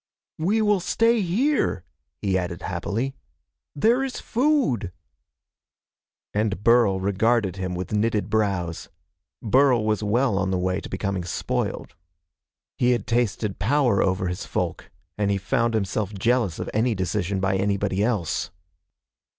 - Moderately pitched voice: No, low, 105 Hz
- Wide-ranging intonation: No, average, 4.5 semitones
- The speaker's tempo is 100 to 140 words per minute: Yes, slow, 135 wpm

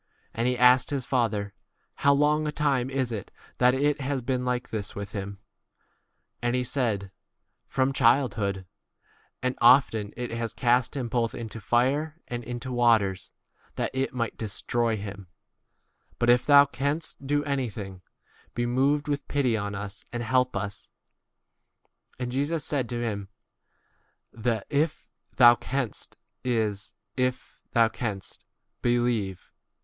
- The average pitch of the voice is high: No, low, 120 Hz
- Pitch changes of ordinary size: Yes, average, 3.3 semitones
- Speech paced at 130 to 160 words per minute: Yes, average, 150 wpm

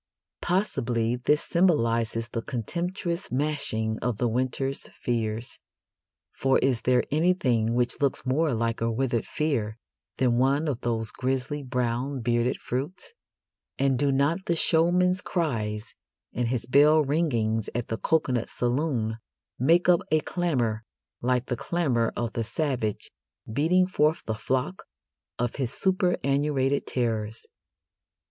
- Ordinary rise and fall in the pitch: Yes, average, 4.7 semitones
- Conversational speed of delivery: No, slow, 130 wpm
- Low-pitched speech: Yes, low, 130 Hz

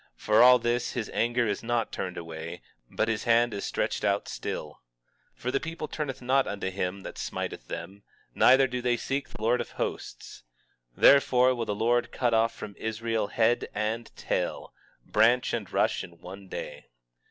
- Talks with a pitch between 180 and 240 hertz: No, low, 115 Hz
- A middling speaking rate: Yes, average, 185 wpm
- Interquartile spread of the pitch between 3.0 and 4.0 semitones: Yes, average, 3.4 semitones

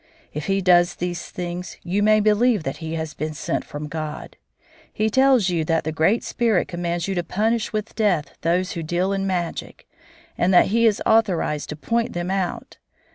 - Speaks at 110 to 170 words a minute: No, average, 190 wpm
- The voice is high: No, medium, 180 Hz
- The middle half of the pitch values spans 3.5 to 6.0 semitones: Yes, average, 4.3 semitones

